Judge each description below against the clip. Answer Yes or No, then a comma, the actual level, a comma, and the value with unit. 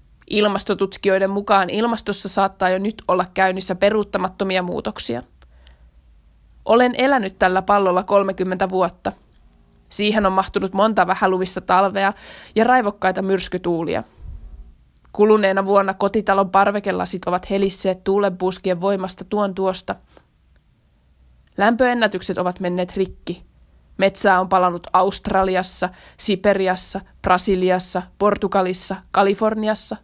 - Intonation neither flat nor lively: No, narrow, 1.7 semitones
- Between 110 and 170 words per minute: No, slow, 95 wpm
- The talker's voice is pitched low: No, high, 190 Hz